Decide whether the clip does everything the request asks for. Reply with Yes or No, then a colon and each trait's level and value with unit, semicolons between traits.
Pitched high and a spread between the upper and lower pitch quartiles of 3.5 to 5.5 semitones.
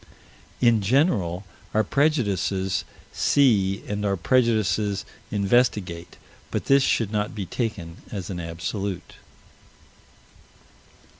No: low, 100 Hz; average, 3.8 semitones